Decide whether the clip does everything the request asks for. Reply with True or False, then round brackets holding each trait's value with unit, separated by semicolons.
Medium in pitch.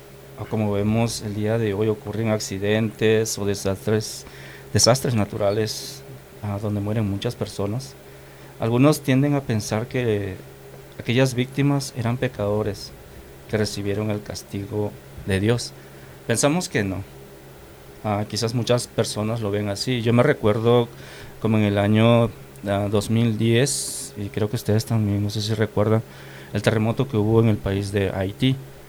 False (105 Hz)